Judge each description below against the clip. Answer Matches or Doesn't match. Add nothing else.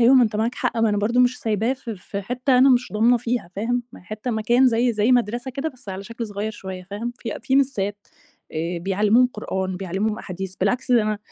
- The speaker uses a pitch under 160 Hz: Doesn't match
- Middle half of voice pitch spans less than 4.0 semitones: Matches